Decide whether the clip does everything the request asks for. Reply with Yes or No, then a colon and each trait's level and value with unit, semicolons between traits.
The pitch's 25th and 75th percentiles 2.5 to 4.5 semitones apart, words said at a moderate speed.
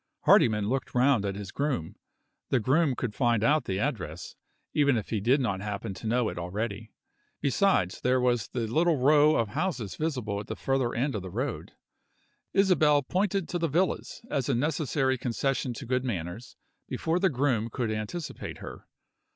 No: average, 5.3 semitones; average, 175 wpm